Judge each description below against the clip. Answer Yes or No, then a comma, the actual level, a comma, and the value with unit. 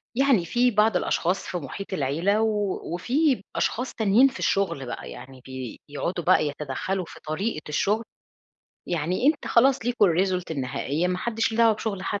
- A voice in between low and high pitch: No, high, 195 Hz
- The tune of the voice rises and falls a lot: Yes, wide, 5.9 semitones